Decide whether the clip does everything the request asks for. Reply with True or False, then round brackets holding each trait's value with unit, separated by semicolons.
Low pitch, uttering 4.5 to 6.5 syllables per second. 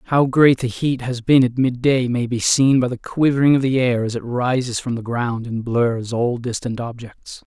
True (125 Hz; 4.6 syllables/s)